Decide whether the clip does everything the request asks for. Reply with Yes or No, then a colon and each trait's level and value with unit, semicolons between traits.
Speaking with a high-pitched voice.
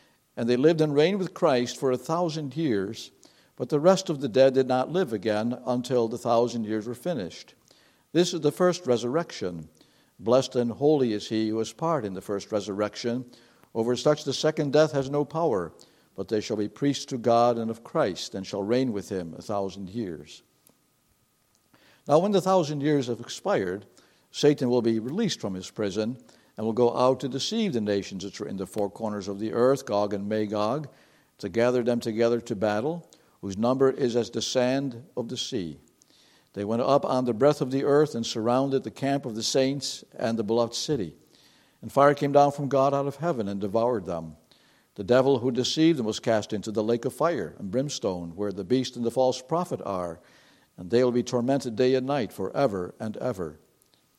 No: low, 125 Hz